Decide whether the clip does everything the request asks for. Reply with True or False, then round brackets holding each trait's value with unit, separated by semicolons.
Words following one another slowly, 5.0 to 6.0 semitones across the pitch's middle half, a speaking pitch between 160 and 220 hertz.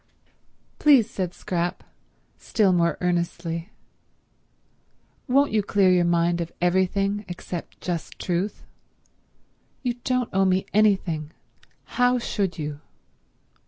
False (105 wpm; 3.2 semitones; 185 Hz)